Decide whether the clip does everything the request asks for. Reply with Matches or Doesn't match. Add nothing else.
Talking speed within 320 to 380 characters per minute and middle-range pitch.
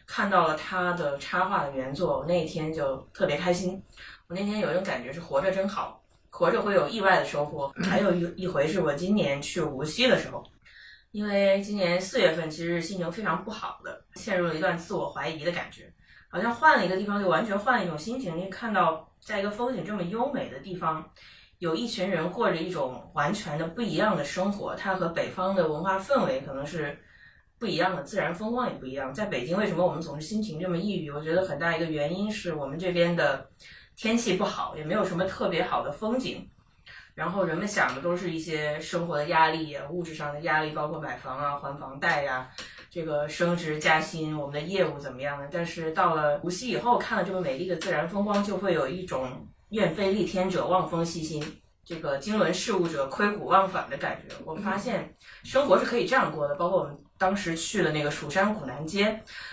Matches